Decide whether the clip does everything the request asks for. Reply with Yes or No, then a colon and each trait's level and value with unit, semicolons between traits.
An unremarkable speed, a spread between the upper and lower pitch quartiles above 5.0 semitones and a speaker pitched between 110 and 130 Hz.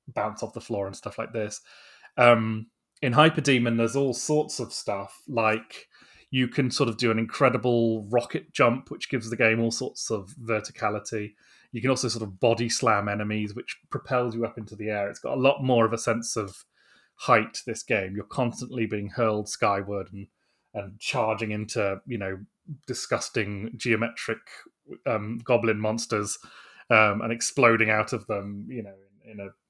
No: average, 180 wpm; average, 2.8 semitones; low, 115 Hz